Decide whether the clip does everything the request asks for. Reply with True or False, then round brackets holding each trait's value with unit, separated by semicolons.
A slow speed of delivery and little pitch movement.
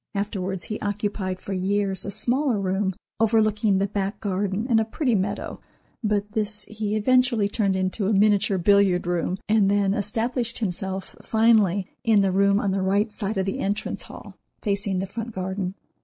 False (170 wpm; 2.0 semitones)